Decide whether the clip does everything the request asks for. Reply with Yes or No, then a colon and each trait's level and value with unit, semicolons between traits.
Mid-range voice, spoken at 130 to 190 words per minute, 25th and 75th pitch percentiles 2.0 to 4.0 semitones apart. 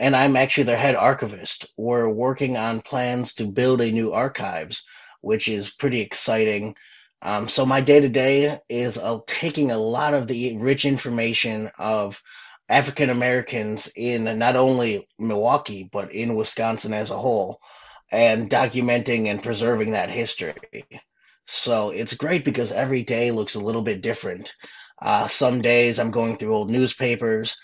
No: low, 120 Hz; average, 155 wpm; average, 2.7 semitones